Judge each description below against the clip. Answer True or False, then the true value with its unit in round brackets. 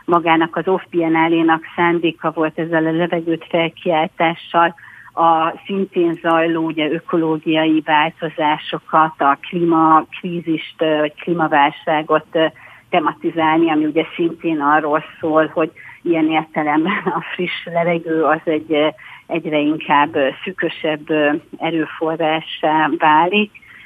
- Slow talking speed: True (100 wpm)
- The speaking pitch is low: False (160 Hz)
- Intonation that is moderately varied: False (1.4 semitones)